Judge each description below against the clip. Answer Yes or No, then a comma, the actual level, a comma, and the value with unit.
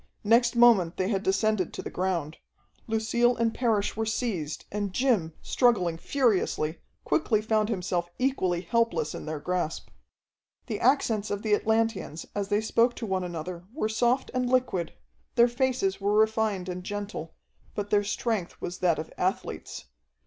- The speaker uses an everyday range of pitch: Yes, average, 4.2 semitones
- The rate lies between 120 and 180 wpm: Yes, average, 155 wpm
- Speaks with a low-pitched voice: No, high, 205 Hz